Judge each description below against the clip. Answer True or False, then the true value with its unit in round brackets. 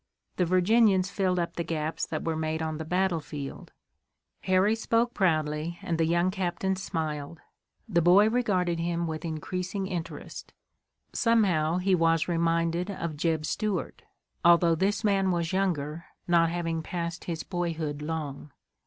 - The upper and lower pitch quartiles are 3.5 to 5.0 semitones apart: False (2.6 semitones)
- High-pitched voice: False (170 Hz)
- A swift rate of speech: False (145 wpm)